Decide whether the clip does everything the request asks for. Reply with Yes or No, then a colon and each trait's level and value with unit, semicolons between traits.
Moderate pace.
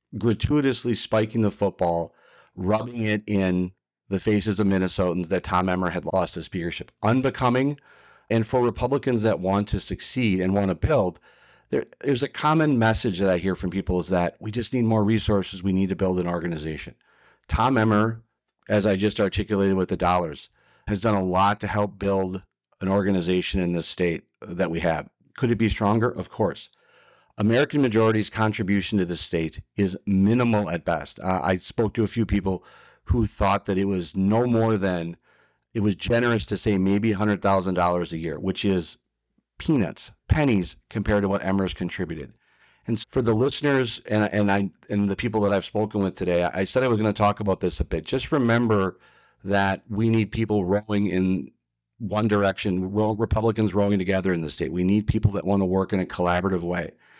Yes: average, 190 wpm